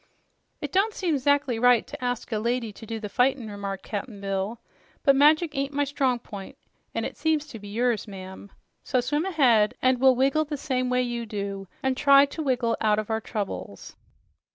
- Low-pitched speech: No, high, 245 Hz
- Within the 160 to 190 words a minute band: No, average, 200 wpm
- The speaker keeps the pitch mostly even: No, average, 4.6 semitones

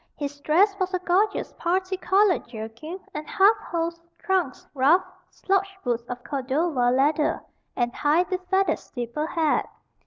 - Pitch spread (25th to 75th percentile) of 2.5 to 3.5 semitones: No, wide, 5.6 semitones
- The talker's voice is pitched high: Yes, very high, 330 Hz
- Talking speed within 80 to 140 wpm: Yes, slow, 135 wpm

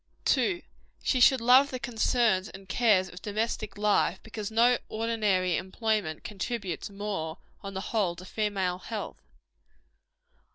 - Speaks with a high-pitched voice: Yes, high, 210 Hz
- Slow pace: Yes, slow, 130 wpm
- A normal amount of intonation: Yes, average, 3.5 semitones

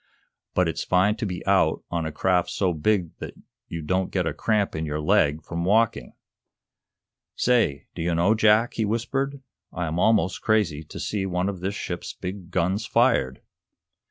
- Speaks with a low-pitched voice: Yes, very low, 95 Hz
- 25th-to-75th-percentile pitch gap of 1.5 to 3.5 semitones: No, average, 4.3 semitones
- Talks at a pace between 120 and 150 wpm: No, average, 180 wpm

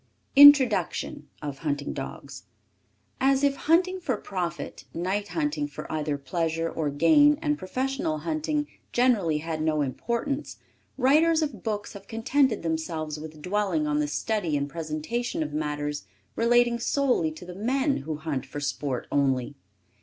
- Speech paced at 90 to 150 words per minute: Yes, average, 140 wpm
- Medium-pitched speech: Yes, medium, 180 Hz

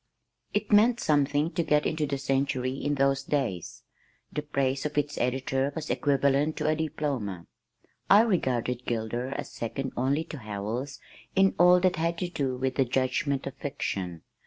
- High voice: No, medium, 140 Hz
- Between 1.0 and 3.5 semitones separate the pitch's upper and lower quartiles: Yes, average, 3.0 semitones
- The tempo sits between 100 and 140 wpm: No, average, 165 wpm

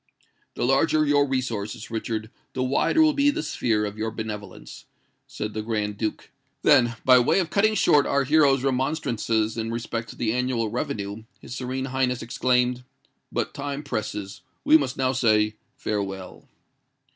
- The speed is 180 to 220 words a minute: No, average, 155 wpm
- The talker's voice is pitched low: Yes, low, 125 Hz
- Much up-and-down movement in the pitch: No, average, 4.0 semitones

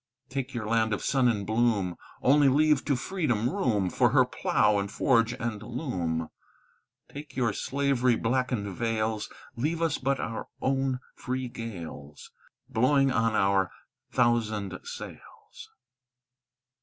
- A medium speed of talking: No, slow, 130 wpm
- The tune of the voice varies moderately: Yes, average, 4.1 semitones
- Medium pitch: No, low, 120 Hz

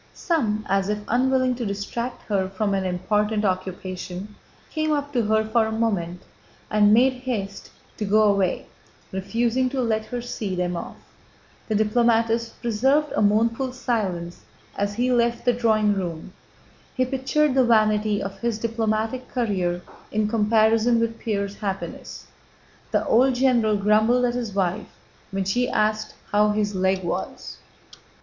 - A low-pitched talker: No, high, 215 Hz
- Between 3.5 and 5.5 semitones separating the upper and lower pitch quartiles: No, average, 3.1 semitones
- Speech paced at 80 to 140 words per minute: No, average, 150 wpm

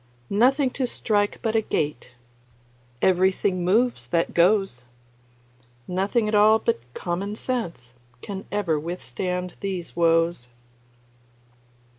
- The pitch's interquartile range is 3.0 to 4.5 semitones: Yes, average, 4.1 semitones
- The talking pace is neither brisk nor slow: No, slow, 105 wpm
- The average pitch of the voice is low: No, high, 190 Hz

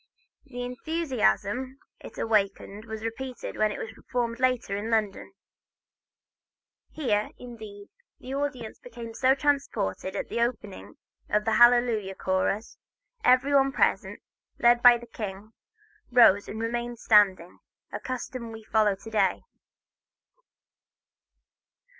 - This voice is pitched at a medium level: No, high, 230 Hz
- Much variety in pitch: No, average, 3.1 semitones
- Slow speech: Yes, slow, 125 wpm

